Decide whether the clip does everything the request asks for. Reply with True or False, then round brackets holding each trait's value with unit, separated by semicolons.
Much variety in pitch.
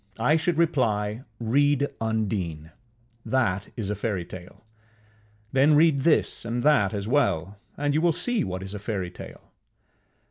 True (6.6 semitones)